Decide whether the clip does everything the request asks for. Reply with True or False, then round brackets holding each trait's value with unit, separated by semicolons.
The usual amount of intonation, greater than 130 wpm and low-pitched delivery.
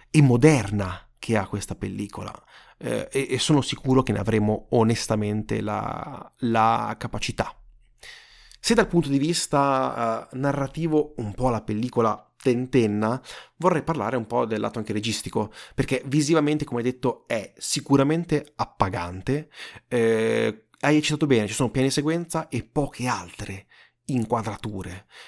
True (5.0 semitones; 140 wpm; 125 Hz)